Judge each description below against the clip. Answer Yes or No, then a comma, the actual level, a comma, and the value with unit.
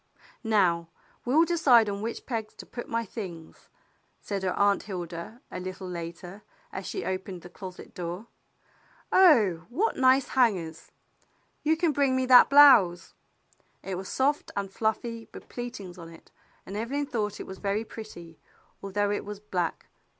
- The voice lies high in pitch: Yes, high, 205 Hz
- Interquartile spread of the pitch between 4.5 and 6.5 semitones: Yes, average, 5.1 semitones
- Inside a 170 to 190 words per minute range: No, average, 155 wpm